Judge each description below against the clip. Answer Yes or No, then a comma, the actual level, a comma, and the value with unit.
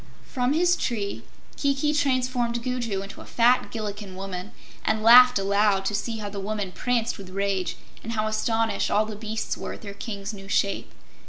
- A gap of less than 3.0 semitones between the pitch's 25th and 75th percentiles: No, average, 3.4 semitones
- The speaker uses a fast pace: No, average, 180 wpm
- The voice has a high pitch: Yes, high, 215 Hz